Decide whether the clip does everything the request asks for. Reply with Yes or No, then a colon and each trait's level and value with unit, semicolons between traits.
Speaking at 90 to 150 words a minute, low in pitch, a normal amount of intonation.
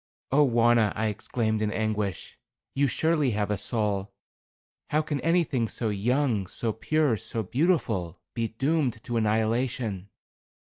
Yes: slow, 135 wpm; low, 115 Hz; average, 4.3 semitones